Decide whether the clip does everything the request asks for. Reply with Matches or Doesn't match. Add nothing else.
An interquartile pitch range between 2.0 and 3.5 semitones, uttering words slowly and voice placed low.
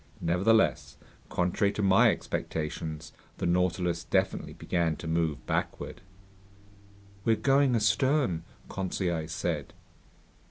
Doesn't match